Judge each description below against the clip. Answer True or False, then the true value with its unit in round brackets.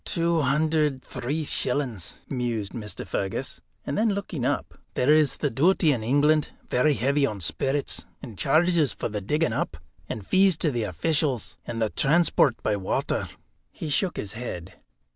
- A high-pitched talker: False (140 Hz)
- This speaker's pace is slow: False (165 wpm)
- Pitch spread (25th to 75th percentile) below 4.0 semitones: False (5.4 semitones)